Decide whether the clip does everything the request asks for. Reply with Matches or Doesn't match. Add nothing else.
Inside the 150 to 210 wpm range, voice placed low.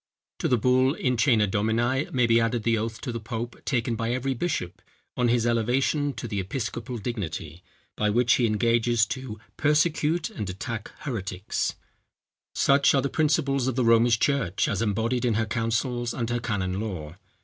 Matches